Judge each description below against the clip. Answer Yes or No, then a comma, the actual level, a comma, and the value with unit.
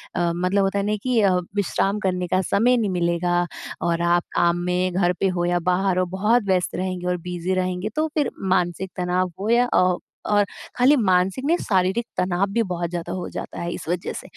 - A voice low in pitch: No, medium, 185 Hz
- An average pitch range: No, narrow, 2.1 semitones